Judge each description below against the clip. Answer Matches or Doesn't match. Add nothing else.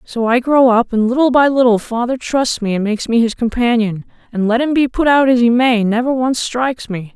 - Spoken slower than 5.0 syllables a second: Doesn't match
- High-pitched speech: Matches